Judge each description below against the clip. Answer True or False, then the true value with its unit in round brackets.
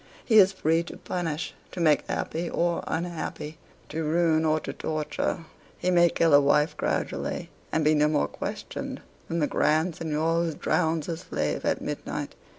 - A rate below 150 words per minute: False (170 wpm)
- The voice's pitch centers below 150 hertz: False (160 Hz)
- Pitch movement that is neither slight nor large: False (1.7 semitones)